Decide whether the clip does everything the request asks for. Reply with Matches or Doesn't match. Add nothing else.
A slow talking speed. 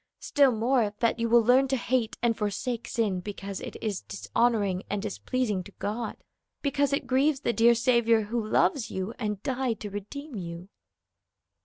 Doesn't match